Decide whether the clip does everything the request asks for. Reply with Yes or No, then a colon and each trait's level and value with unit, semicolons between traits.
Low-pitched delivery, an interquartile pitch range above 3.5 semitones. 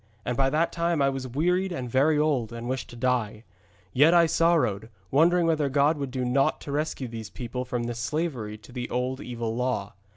Yes: low, 130 Hz; average, 4.3 semitones